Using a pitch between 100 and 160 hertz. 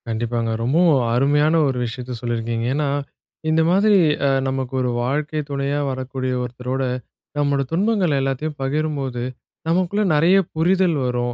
Yes: medium, 140 Hz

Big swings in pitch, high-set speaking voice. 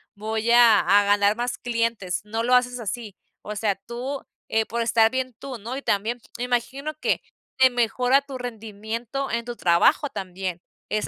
No: average, 2.8 semitones; high, 230 Hz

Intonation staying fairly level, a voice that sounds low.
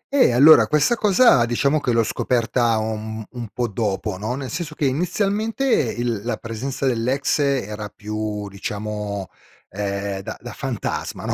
No: average, 4.7 semitones; low, 120 Hz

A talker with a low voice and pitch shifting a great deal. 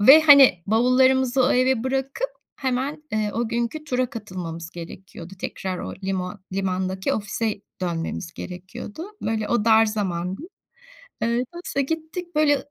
No: high, 225 Hz; wide, 5.9 semitones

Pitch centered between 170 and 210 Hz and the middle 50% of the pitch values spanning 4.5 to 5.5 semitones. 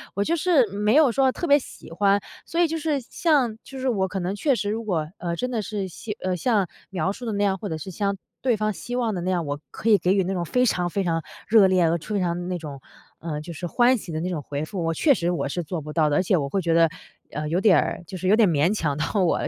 Yes: high, 190 Hz; average, 5.0 semitones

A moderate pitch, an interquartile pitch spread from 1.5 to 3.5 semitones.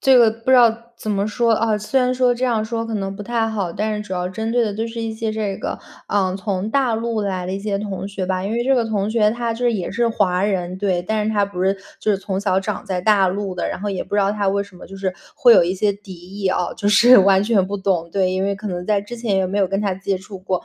No: high, 205 Hz; average, 2.7 semitones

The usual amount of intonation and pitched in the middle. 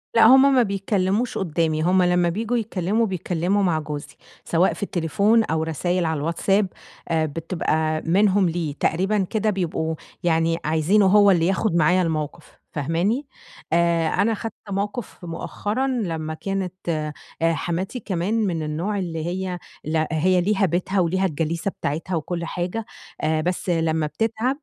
Yes: average, 3.7 semitones; medium, 175 Hz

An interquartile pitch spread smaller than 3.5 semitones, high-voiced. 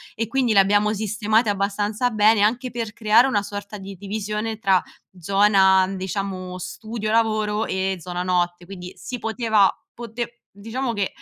Yes: narrow, 2.5 semitones; high, 210 Hz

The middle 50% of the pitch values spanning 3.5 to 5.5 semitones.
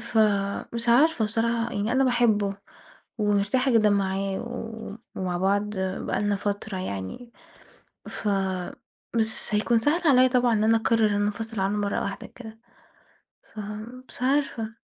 No: average, 2.7 semitones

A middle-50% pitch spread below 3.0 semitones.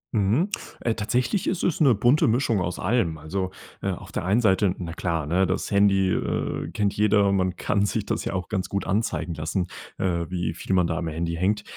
No: average, 3.3 semitones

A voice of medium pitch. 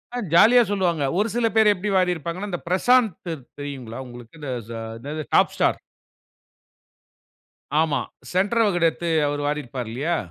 Yes: medium, 170 Hz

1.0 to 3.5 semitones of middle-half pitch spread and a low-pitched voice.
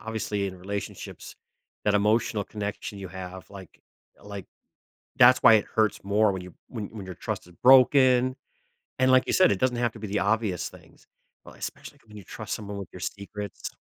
Yes: narrow, 2.5 semitones; low, 105 Hz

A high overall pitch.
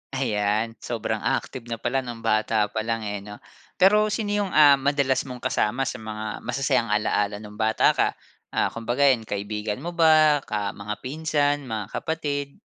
No: low, 120 Hz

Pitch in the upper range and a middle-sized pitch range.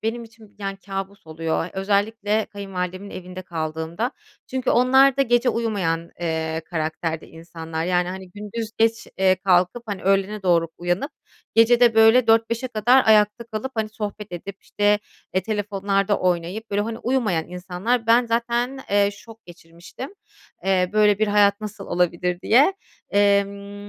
Yes: high, 200 Hz; average, 3.9 semitones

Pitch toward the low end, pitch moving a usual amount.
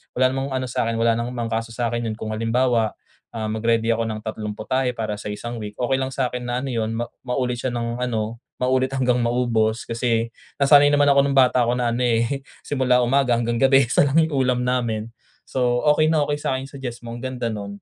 No: low, 120 Hz; narrow, 2.2 semitones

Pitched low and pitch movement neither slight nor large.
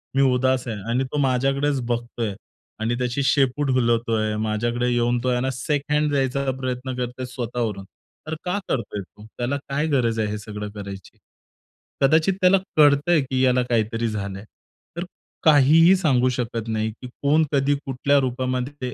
Yes: low, 125 Hz; average, 3.1 semitones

